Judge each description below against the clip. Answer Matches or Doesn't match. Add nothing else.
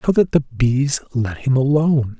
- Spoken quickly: Doesn't match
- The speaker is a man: Matches